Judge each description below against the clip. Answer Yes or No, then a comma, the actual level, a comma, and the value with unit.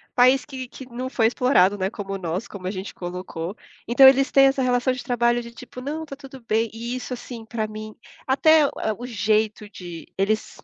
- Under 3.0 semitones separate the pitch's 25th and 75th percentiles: No, average, 3.7 semitones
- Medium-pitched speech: No, high, 235 Hz